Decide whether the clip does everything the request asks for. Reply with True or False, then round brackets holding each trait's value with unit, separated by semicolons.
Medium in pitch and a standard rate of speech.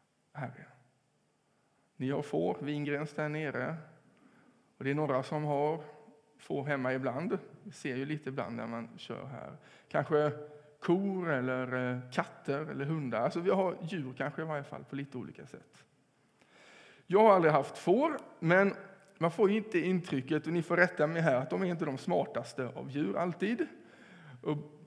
True (150 Hz; 165 wpm)